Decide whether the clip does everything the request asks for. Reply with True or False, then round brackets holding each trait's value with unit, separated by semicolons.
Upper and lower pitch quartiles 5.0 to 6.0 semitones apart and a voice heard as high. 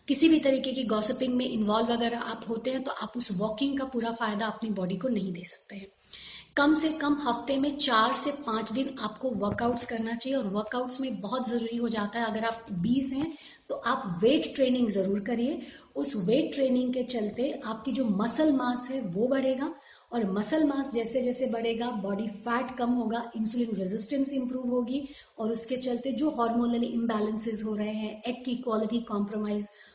False (3.3 semitones; 240 Hz)